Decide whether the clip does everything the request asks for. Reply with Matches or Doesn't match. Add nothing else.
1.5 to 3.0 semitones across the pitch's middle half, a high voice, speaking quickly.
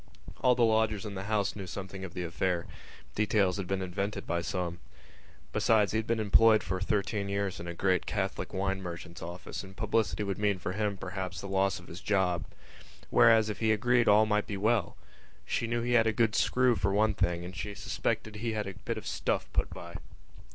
Doesn't match